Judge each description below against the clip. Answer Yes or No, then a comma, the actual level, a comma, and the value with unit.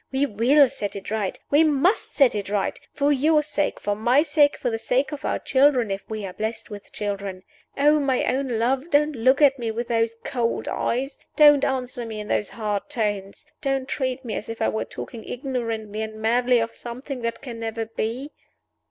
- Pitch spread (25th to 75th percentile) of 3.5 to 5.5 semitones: Yes, average, 4.0 semitones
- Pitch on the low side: No, high, 240 Hz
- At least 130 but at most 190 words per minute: No, fast, 205 wpm